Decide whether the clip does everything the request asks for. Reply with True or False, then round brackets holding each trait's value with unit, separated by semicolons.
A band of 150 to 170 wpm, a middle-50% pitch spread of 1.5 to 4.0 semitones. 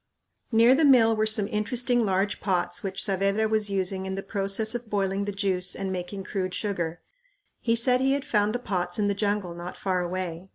False (205 wpm; 2.7 semitones)